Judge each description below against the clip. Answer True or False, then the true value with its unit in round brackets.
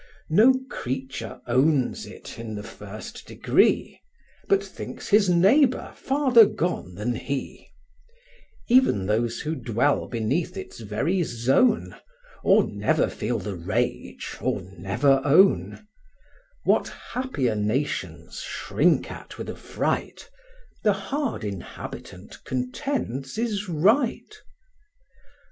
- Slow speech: True (105 wpm)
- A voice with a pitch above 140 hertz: False (135 Hz)